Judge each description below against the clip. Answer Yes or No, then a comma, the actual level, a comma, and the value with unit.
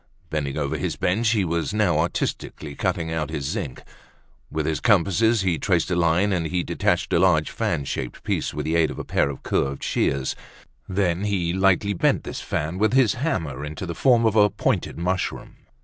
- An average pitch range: Yes, average, 4.5 semitones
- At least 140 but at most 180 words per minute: No, average, 195 wpm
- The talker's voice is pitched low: Yes, very low, 90 Hz